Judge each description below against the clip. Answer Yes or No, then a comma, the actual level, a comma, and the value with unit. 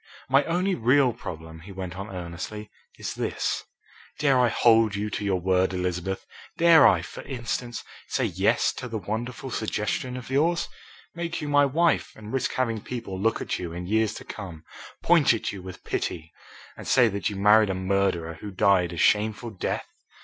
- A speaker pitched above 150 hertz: No, low, 105 Hz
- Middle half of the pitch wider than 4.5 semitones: Yes, average, 5.1 semitones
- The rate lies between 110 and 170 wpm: No, average, 185 wpm